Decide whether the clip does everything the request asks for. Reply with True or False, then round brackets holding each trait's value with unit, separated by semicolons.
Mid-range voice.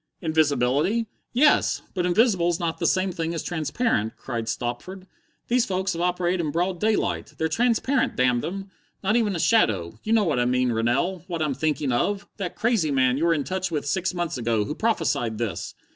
True (170 Hz)